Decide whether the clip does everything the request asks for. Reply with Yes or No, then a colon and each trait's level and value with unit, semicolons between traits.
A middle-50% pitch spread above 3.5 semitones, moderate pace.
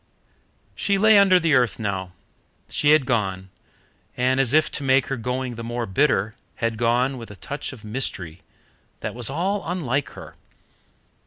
Yes: average, 4.6 semitones; average, 165 wpm